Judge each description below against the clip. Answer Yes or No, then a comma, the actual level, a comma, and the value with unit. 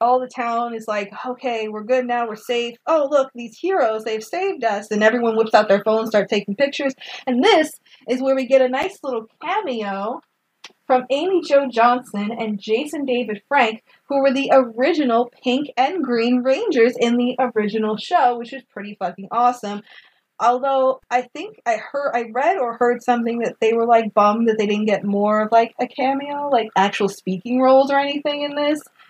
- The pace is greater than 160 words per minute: Yes, average, 195 wpm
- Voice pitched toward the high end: Yes, high, 245 Hz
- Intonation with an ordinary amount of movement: Yes, average, 3.5 semitones